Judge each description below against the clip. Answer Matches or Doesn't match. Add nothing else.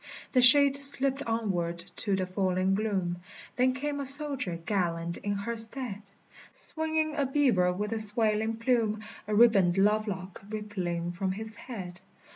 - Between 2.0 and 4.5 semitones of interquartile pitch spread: Doesn't match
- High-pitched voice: Matches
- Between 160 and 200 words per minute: Doesn't match